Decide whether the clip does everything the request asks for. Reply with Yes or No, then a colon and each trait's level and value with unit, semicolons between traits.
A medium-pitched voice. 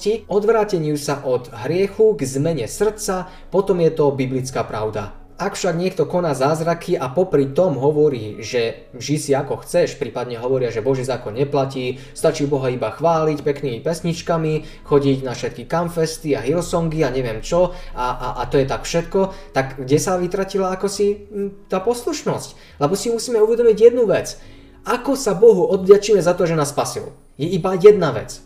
Yes: medium, 160 Hz